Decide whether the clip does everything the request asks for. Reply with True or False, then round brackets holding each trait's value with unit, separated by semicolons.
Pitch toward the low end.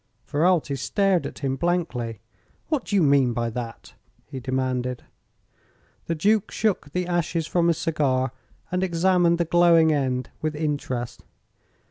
False (155 Hz)